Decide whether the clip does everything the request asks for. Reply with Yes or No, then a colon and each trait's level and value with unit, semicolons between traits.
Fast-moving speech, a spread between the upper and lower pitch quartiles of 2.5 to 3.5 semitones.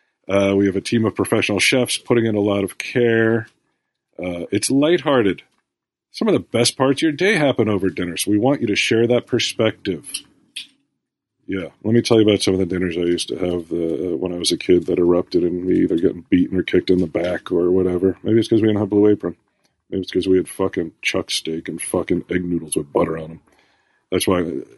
No: fast, 235 wpm; average, 4.1 semitones